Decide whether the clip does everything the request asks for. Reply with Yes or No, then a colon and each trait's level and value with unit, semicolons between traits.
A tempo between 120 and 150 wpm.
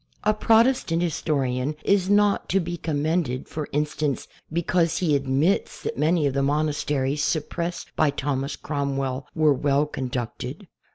Yes: slow, 135 wpm